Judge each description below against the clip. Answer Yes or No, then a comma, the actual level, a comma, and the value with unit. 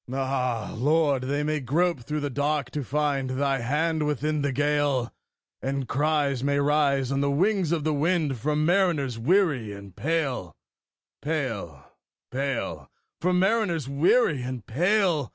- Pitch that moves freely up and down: No, average, 3.1 semitones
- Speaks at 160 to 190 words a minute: No, average, 145 wpm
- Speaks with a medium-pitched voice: Yes, medium, 145 Hz